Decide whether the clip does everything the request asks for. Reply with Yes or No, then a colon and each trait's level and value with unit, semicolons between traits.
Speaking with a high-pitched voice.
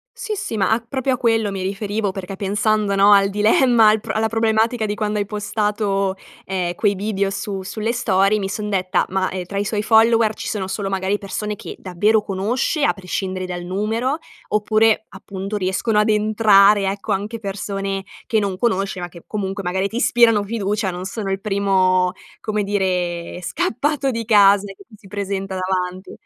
Yes: high, 205 Hz